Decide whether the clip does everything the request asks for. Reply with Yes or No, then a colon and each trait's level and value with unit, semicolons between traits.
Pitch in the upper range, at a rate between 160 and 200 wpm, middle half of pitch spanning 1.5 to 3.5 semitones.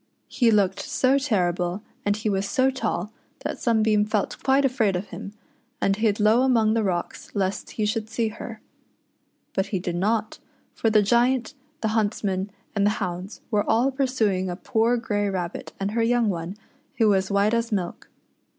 Yes: high, 215 Hz; average, 180 wpm; average, 2.8 semitones